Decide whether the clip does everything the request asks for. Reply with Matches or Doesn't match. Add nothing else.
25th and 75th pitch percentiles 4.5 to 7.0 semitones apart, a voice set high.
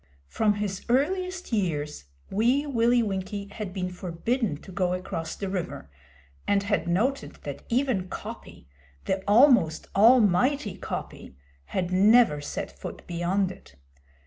Matches